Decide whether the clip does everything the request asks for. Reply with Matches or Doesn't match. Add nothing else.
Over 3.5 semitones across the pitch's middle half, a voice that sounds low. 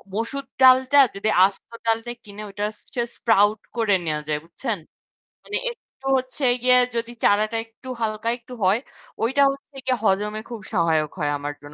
Doesn't match